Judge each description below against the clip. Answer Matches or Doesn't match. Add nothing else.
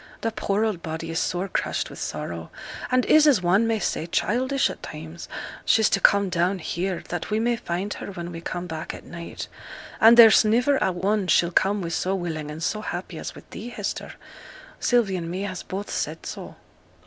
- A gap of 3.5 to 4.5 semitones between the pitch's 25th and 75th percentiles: Matches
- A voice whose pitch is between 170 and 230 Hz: Matches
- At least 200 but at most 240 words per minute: Matches